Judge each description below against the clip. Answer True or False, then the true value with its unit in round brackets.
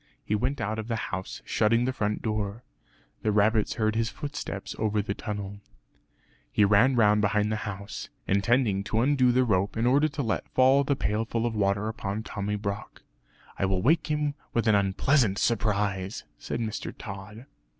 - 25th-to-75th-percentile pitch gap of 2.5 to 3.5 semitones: True (2.9 semitones)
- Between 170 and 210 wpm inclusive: True (180 wpm)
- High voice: False (110 Hz)